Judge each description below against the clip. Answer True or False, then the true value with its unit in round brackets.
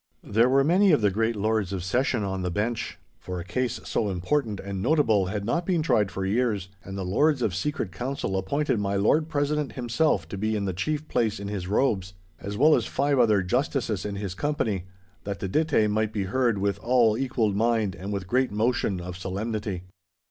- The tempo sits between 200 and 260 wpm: True (205 wpm)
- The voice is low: True (110 Hz)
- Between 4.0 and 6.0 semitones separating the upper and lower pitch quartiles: True (4.7 semitones)